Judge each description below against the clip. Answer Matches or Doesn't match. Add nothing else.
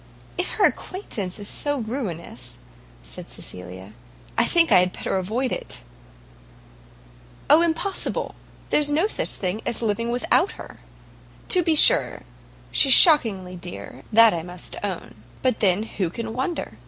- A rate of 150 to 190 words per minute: Doesn't match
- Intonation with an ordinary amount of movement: Doesn't match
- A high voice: Matches